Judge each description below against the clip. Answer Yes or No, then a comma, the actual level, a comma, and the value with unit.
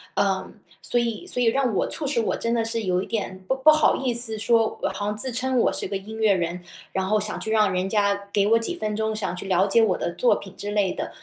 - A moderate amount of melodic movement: Yes, average, 3.0 semitones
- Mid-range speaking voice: No, high, 215 Hz